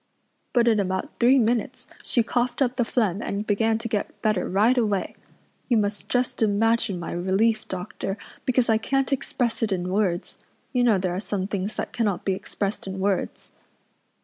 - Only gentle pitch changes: No, average, 3.6 semitones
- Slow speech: No, average, 180 wpm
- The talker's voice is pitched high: Yes, high, 215 Hz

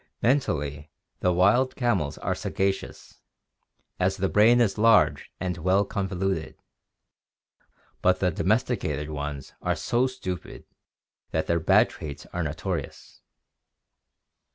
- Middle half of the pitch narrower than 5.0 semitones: No, wide, 5.4 semitones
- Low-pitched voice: Yes, very low, 95 Hz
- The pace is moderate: No, slow, 115 wpm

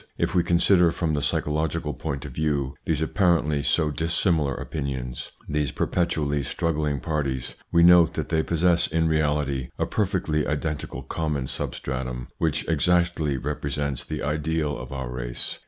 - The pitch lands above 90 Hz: No, very low, 75 Hz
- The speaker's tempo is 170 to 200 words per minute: No, average, 150 wpm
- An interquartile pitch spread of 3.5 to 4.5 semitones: No, average, 2.8 semitones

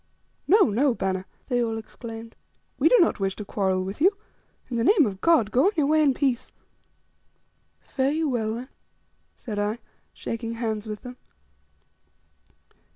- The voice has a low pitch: No, high, 230 Hz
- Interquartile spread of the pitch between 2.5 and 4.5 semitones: No, average, 5.0 semitones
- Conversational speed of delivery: Yes, average, 160 wpm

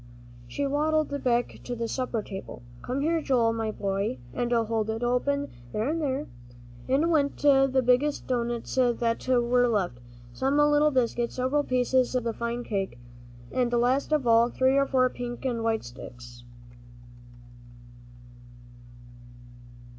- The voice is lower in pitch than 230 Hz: No, high, 245 Hz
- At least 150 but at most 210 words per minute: No, average, 140 wpm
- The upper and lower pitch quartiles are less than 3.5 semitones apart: Yes, average, 3.1 semitones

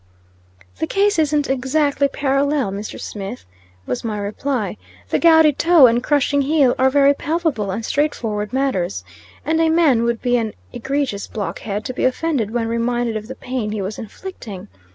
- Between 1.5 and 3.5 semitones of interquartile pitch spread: No, average, 5.1 semitones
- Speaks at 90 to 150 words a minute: No, average, 165 wpm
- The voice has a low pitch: No, very high, 255 Hz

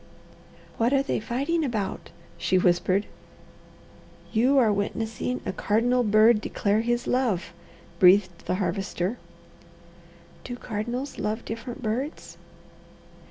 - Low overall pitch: No, high, 225 Hz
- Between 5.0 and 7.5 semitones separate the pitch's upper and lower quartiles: No, average, 3.5 semitones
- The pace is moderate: No, slow, 110 wpm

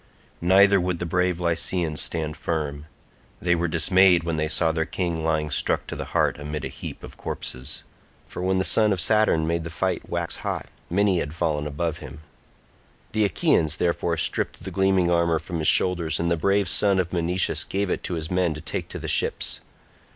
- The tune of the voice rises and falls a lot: No, narrow, 2.5 semitones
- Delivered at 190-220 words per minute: Yes, average, 195 wpm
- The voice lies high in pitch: No, very low, 85 Hz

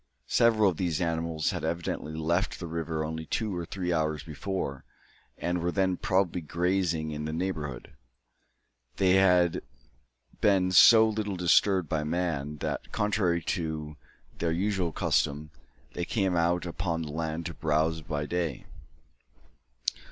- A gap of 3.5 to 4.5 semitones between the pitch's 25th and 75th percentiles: No, average, 2.7 semitones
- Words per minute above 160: No, average, 140 wpm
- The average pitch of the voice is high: No, very low, 85 Hz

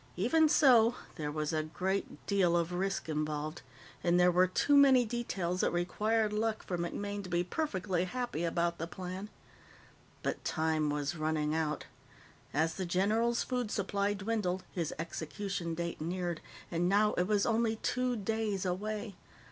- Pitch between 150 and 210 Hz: Yes, medium, 185 Hz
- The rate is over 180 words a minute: No, average, 155 wpm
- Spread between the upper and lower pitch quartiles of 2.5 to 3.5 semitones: No, average, 4.0 semitones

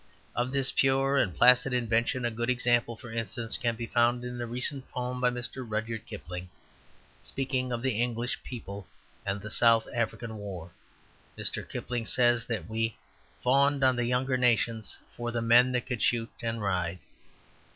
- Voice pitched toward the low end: Yes, low, 120 Hz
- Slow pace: No, average, 170 wpm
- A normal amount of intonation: No, narrow, 1.8 semitones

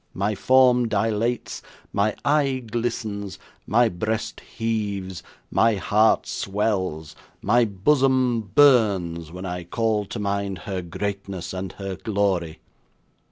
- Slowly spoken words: Yes, slow, 115 wpm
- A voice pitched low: Yes, low, 105 Hz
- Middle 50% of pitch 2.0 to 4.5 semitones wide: Yes, average, 3.3 semitones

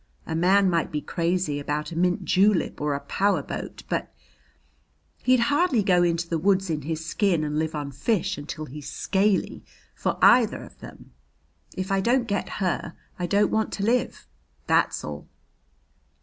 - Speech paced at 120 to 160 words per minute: No, average, 170 wpm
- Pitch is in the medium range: Yes, medium, 180 Hz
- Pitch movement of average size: Yes, average, 4.5 semitones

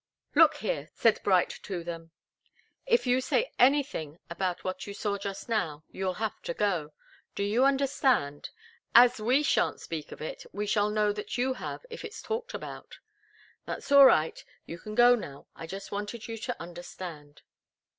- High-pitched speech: Yes, high, 210 Hz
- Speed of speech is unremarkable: Yes, average, 175 wpm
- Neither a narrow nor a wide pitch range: No, wide, 6.6 semitones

